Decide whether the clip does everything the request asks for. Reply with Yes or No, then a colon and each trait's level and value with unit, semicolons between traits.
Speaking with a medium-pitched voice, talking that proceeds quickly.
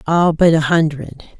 No: medium, 160 Hz; average, 170 wpm